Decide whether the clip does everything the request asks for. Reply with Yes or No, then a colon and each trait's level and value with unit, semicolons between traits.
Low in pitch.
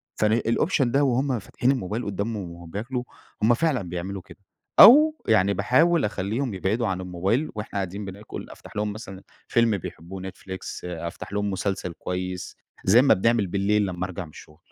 Yes: low, 100 Hz